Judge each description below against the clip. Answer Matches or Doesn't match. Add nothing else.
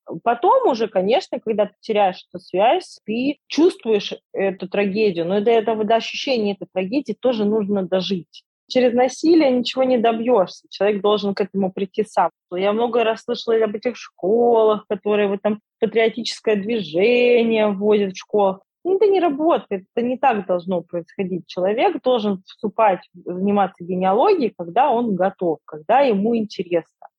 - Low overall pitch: Doesn't match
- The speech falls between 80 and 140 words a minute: Doesn't match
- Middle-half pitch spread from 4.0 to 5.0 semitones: Doesn't match